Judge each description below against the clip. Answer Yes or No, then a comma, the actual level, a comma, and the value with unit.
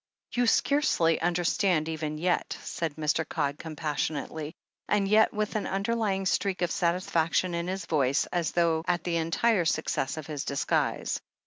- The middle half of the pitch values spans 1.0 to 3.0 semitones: No, average, 3.4 semitones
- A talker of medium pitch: Yes, medium, 170 Hz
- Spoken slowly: No, average, 150 wpm